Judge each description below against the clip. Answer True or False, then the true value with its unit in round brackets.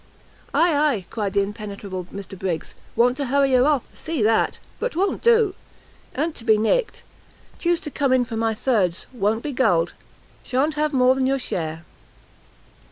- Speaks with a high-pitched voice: True (250 Hz)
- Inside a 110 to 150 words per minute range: False (175 wpm)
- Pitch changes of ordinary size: False (6.1 semitones)